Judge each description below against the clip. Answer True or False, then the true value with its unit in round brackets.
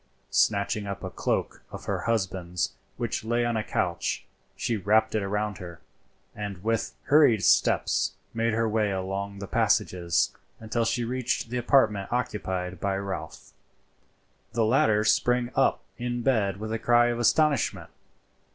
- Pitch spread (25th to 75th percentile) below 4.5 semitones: True (3.2 semitones)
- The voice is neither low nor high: False (110 Hz)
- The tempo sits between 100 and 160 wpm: True (150 wpm)